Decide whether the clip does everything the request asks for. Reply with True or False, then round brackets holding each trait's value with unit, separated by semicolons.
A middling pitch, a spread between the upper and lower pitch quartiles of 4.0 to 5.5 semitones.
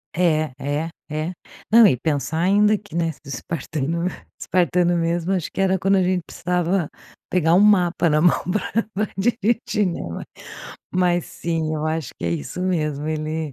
False (170 Hz; 3.2 semitones)